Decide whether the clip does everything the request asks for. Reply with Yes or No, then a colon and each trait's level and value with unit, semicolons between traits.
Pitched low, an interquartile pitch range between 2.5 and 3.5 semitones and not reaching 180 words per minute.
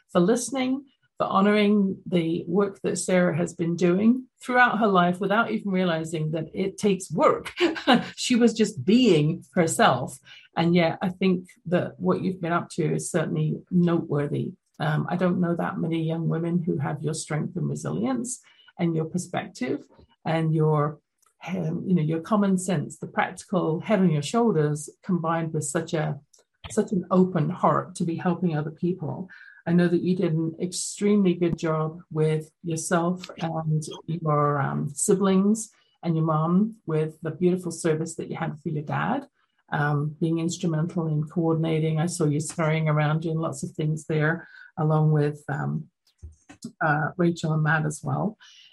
No: medium, 170 Hz; average, 3.2 semitones; average, 165 wpm